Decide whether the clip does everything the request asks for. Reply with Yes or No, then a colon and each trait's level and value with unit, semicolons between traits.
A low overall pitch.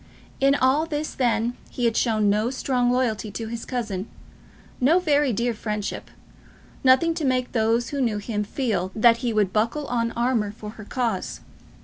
No: high, 235 Hz